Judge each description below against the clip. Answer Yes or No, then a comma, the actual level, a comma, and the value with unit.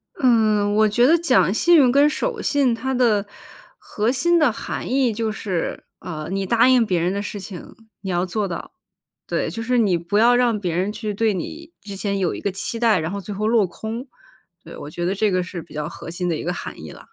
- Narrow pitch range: No, average, 4.6 semitones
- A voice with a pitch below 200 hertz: No, high, 210 Hz